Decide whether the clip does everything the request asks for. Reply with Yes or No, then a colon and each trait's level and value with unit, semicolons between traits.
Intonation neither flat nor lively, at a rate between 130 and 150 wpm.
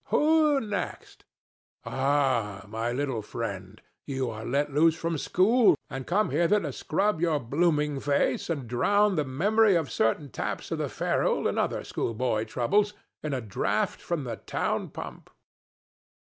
No: wide, 6.7 semitones; average, 145 wpm